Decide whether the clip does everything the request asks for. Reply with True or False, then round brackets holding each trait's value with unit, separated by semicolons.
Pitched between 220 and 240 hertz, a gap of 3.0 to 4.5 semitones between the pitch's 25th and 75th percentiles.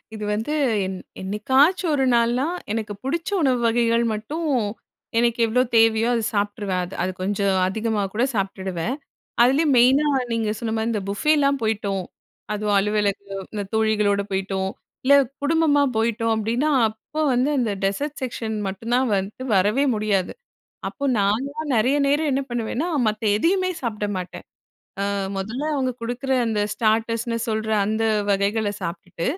True (225 Hz; 4.0 semitones)